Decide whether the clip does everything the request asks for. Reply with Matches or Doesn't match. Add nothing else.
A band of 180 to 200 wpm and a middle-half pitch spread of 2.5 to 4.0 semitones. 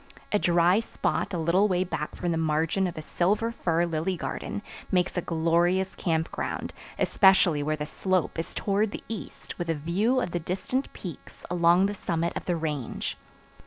Matches